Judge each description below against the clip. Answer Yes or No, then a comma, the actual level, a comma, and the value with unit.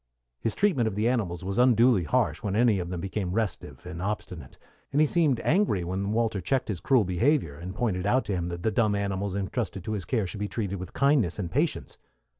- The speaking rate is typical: No, fast, 225 wpm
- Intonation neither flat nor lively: Yes, average, 4.6 semitones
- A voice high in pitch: No, low, 100 Hz